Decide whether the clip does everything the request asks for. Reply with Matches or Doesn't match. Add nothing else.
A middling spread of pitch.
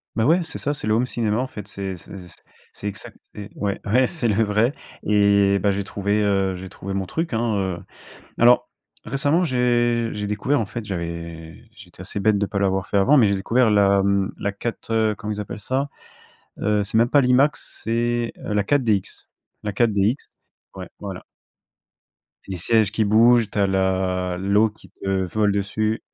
Matches